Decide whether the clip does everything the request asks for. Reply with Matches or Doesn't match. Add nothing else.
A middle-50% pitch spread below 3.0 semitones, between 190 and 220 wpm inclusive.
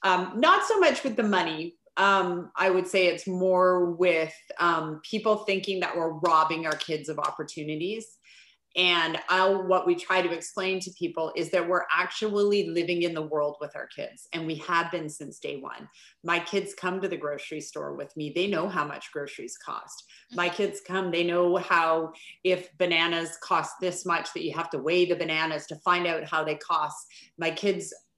Matches